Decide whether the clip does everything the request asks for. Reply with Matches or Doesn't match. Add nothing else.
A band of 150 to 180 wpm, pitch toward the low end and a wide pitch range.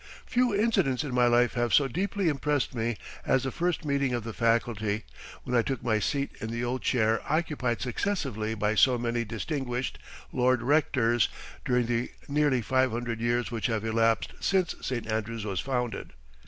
Doesn't match